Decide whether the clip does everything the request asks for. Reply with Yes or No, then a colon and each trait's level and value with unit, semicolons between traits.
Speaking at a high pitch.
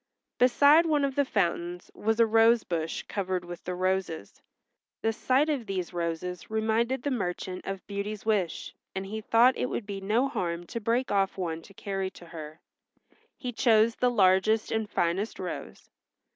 Yes: high, 205 Hz